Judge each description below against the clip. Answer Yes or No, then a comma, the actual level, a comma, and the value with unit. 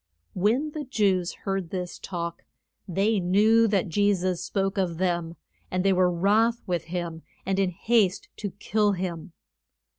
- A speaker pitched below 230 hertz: Yes, high, 190 Hz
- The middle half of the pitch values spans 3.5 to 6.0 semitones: No, narrow, 2.6 semitones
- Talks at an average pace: Yes, average, 155 wpm